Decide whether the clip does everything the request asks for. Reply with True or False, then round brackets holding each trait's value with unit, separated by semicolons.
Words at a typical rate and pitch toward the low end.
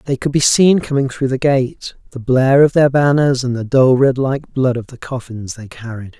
False (215 wpm; 130 Hz)